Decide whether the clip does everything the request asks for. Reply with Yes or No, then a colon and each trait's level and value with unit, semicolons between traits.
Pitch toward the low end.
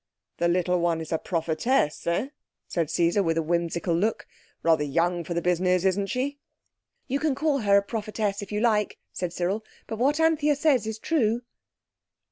No: high, 195 Hz